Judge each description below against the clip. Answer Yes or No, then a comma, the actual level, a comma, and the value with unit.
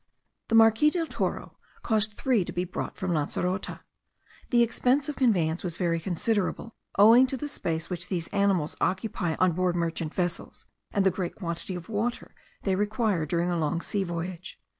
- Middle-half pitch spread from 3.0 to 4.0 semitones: No, average, 4.4 semitones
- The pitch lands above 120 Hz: Yes, medium, 185 Hz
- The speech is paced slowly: No, average, 175 wpm